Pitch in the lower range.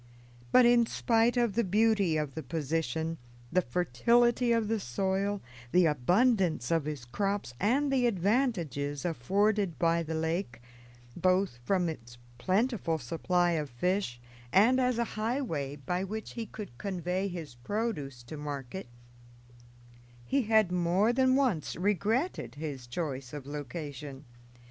No: medium, 180 Hz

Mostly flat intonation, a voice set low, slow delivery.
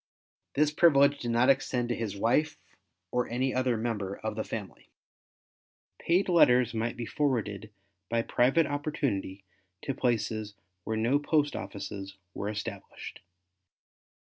No: average, 4.5 semitones; low, 120 Hz; slow, 130 wpm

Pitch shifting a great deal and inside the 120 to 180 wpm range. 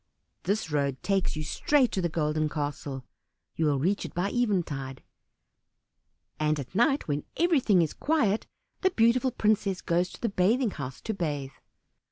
Yes: wide, 7.0 semitones; average, 160 wpm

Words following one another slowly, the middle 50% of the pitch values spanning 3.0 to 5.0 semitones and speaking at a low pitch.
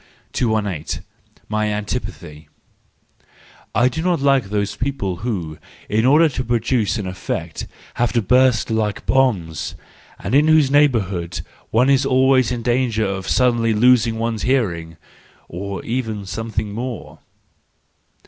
Yes: slow, 125 wpm; average, 4.1 semitones; low, 115 Hz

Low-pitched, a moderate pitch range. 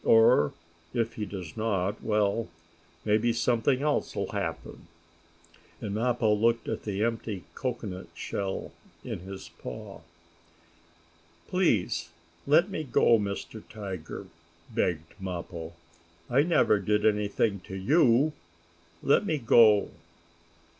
Yes: low, 110 Hz; average, 3.4 semitones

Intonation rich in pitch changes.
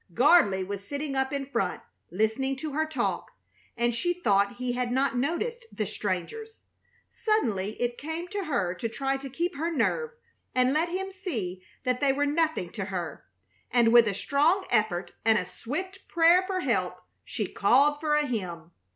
Yes: wide, 7.2 semitones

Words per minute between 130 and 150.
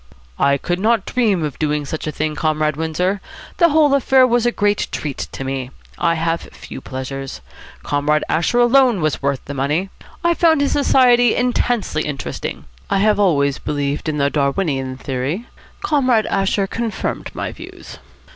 No: average, 165 wpm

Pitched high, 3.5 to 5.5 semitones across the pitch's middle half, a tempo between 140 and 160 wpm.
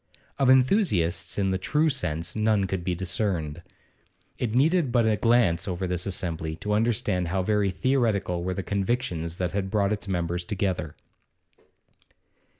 No: very low, 95 Hz; average, 4.1 semitones; average, 150 wpm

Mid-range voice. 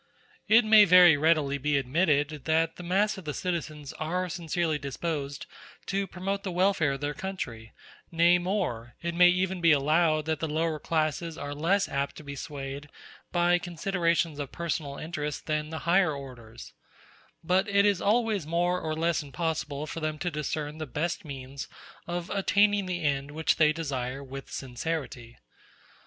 Yes: medium, 160 Hz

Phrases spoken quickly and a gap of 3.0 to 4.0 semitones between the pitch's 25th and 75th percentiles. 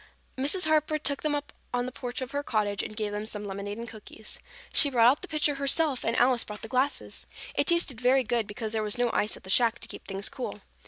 No: fast, 250 wpm; average, 4.7 semitones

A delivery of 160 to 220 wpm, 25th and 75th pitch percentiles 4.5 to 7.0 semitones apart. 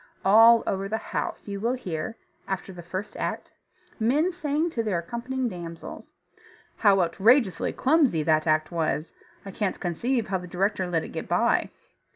Yes: average, 165 wpm; average, 5.3 semitones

